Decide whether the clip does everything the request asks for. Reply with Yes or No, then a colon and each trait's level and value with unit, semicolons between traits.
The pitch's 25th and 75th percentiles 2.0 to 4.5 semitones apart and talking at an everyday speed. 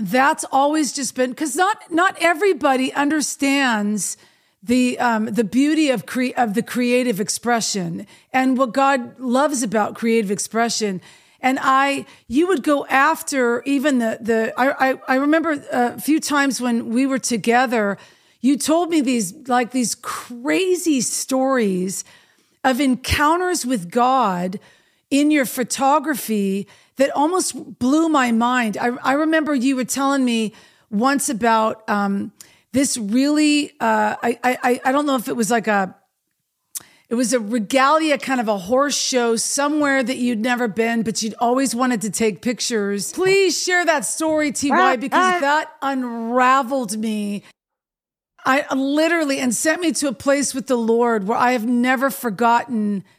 Yes: average, 3.4 semitones; average, 150 wpm